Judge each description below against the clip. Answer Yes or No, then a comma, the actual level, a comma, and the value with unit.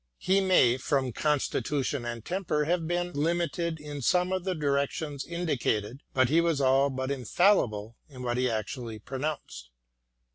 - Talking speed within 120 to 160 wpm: Yes, average, 150 wpm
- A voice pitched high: No, medium, 140 Hz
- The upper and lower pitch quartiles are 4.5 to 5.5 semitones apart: Yes, average, 5.0 semitones